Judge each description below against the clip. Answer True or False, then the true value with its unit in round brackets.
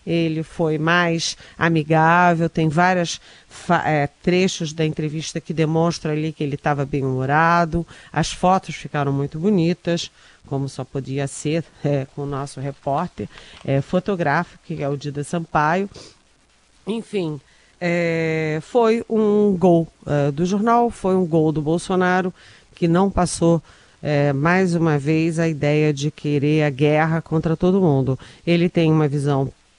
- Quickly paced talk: False (135 wpm)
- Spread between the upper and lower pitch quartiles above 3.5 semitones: False (3.0 semitones)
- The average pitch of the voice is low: False (160 Hz)